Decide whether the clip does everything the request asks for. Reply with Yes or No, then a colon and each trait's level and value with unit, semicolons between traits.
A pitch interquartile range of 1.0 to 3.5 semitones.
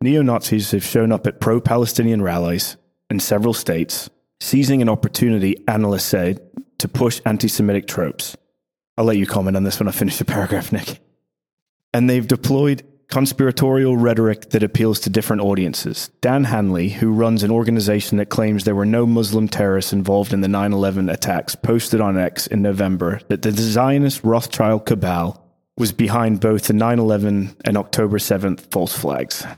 Yes: average, 2.9 semitones